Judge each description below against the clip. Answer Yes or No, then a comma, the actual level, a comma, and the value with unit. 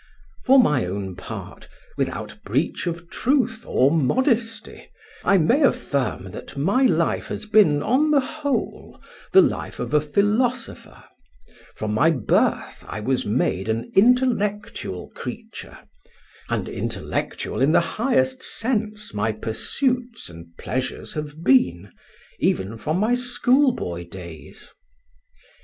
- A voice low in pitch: No, medium, 170 Hz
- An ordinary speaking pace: No, slow, 120 wpm